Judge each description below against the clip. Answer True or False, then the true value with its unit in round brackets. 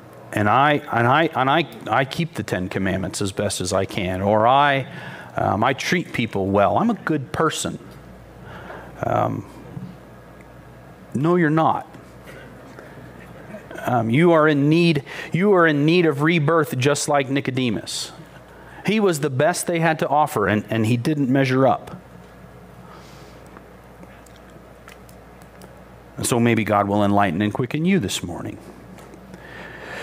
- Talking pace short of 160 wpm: True (140 wpm)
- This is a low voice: True (130 Hz)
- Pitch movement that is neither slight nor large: False (8.5 semitones)